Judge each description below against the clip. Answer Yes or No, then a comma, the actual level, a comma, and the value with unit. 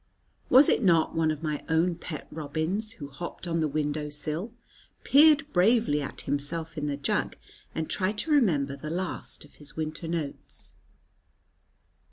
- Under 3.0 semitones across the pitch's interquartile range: No, average, 3.9 semitones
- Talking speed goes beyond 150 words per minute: Yes, average, 160 wpm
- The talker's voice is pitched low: No, medium, 160 Hz